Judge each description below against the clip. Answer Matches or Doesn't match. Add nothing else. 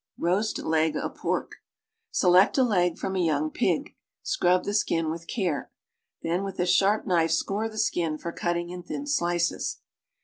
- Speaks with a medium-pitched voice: Matches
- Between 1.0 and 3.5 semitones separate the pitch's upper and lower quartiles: Matches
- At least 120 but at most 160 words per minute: Doesn't match